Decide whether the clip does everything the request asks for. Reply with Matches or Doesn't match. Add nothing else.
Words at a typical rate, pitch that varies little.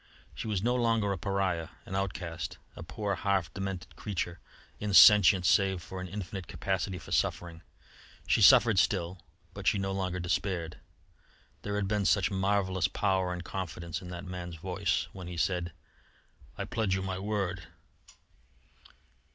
Matches